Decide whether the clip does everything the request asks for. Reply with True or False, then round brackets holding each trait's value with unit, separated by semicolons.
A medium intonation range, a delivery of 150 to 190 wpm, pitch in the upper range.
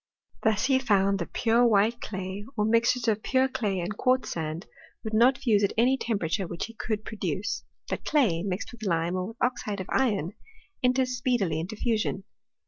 True (4.1 semitones; 185 wpm; 215 Hz)